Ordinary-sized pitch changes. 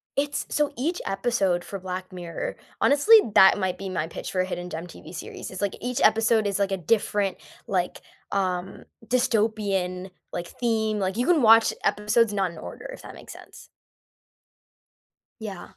Yes: average, 3.6 semitones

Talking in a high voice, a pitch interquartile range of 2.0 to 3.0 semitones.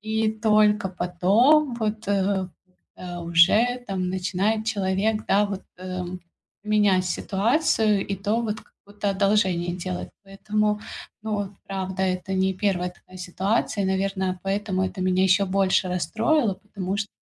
Yes: high, 195 Hz; narrow, 2.4 semitones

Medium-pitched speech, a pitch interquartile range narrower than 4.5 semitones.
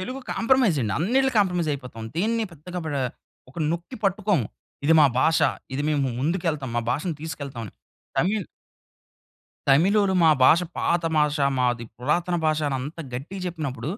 No: medium, 160 Hz; average, 5.1 semitones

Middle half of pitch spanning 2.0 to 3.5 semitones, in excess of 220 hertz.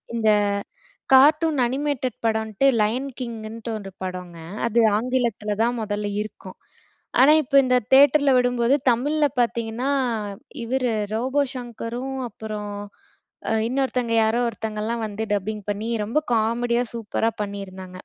Yes: average, 3.1 semitones; high, 230 Hz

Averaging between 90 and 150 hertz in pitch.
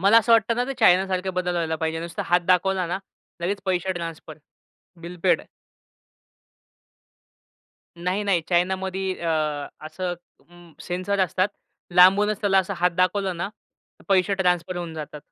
No: medium, 185 Hz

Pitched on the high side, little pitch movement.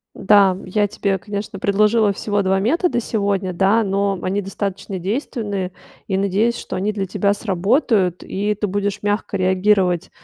Yes: high, 200 Hz; narrow, 1.7 semitones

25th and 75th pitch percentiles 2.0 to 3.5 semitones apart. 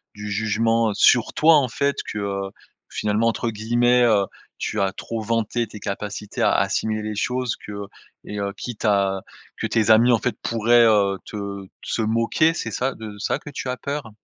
Yes: narrow, 2.5 semitones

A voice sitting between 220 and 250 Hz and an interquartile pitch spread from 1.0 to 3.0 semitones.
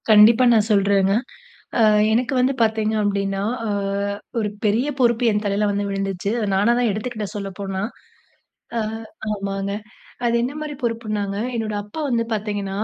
No: high, 210 Hz; narrow, 2.6 semitones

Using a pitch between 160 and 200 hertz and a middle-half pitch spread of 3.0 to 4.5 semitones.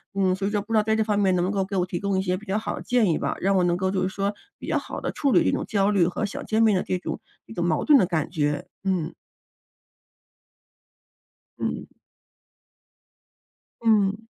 No: high, 195 Hz; narrow, 2.6 semitones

